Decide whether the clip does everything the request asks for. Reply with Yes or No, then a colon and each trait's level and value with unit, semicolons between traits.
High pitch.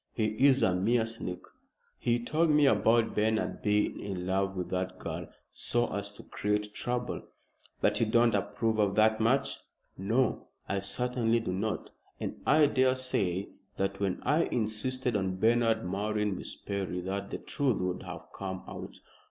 No: low, 105 Hz